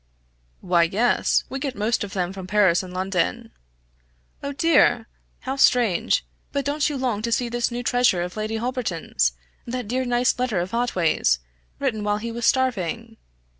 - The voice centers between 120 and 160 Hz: No, high, 230 Hz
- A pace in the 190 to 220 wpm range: No, average, 170 wpm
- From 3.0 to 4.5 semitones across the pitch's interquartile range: No, average, 4.9 semitones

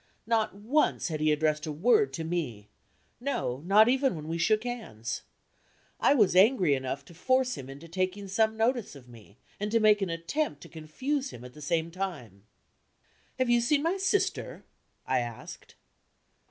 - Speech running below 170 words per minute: No, average, 175 wpm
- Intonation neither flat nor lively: No, wide, 8.0 semitones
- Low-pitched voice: No, medium, 185 Hz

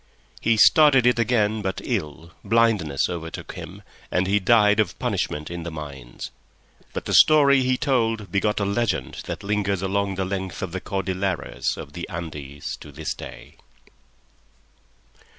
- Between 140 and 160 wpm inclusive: Yes, average, 150 wpm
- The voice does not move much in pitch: No, average, 4.7 semitones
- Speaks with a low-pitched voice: Yes, low, 100 Hz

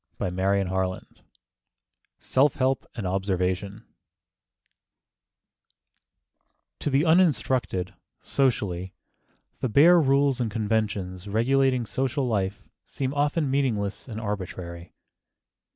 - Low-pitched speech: Yes, low, 110 Hz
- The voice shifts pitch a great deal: Yes, wide, 6.1 semitones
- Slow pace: Yes, slow, 90 wpm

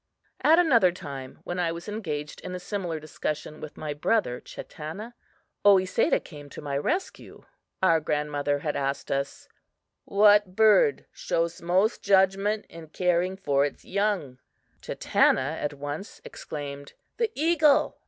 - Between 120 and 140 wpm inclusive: Yes, slow, 135 wpm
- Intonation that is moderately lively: No, wide, 5.8 semitones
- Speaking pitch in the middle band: Yes, medium, 175 Hz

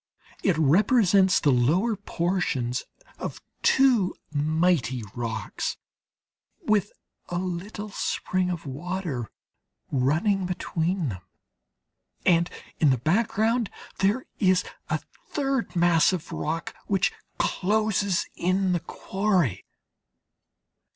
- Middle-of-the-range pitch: Yes, medium, 180 Hz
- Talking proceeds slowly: Yes, slow, 95 wpm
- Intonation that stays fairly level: No, average, 4.5 semitones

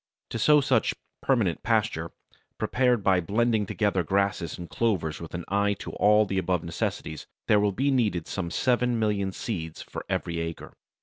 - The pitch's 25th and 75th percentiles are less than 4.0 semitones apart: No, average, 4.8 semitones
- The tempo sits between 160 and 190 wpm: Yes, average, 170 wpm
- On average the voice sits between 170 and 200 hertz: No, low, 100 Hz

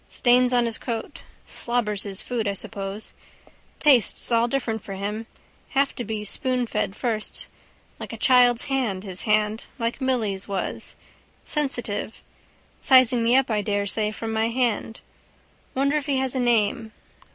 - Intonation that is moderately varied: Yes, average, 3.2 semitones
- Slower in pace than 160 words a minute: Yes, average, 150 wpm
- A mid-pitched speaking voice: No, high, 230 Hz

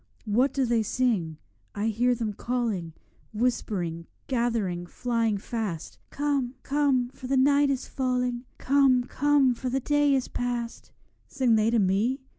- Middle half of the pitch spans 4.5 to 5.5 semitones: No, average, 3.4 semitones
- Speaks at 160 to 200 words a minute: No, average, 145 wpm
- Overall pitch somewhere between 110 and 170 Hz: No, high, 245 Hz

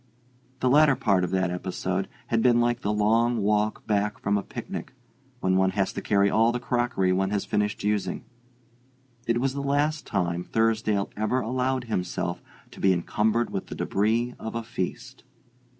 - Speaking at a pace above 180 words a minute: No, average, 175 wpm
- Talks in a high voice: No, low, 105 Hz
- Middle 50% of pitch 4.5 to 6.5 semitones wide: No, average, 3.7 semitones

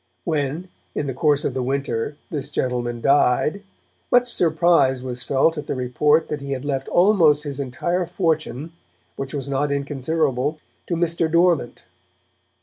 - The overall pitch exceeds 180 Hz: No, medium, 145 Hz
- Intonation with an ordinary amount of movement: Yes, average, 3.6 semitones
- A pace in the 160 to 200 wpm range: No, average, 150 wpm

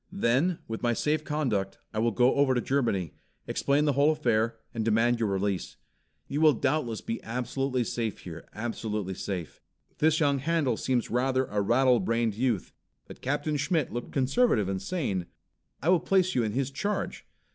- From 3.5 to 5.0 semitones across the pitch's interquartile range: Yes, average, 4.6 semitones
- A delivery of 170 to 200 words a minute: Yes, average, 175 wpm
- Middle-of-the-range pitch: No, low, 125 Hz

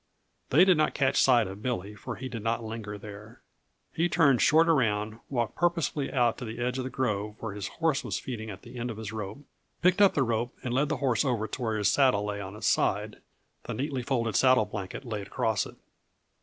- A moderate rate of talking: No, fast, 225 wpm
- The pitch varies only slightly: No, average, 4.1 semitones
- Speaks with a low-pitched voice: Yes, low, 120 Hz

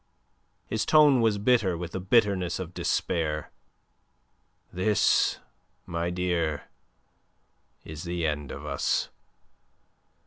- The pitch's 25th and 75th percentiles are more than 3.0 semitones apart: Yes, average, 4.1 semitones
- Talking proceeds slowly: Yes, slow, 100 wpm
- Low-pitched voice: Yes, very low, 90 Hz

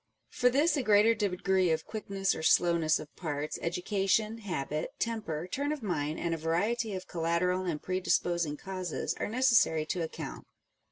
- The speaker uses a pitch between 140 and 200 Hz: Yes, medium, 185 Hz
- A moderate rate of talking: Yes, average, 160 wpm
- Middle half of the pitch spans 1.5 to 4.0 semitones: No, average, 4.8 semitones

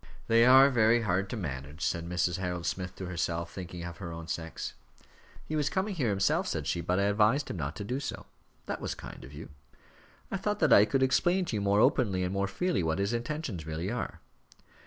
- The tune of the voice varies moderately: No, wide, 5.7 semitones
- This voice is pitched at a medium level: No, low, 100 Hz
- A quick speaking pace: Yes, fast, 225 wpm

